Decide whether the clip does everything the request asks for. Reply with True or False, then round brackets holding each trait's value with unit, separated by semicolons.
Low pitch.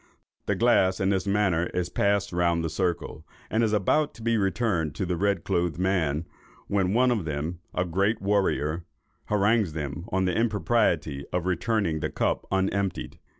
True (95 Hz)